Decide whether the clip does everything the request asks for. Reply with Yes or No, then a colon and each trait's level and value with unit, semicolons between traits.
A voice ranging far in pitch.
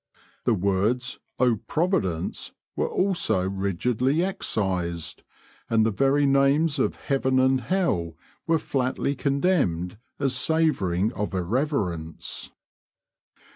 Yes: wide, 7.0 semitones